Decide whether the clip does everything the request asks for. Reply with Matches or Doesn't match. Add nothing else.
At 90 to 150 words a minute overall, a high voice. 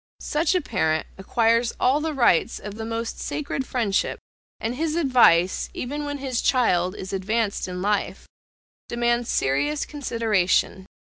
Matches